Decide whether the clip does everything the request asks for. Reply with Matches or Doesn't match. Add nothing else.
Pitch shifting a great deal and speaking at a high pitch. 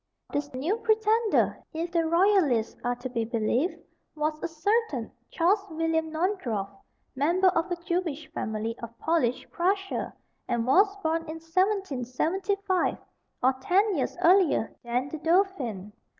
Matches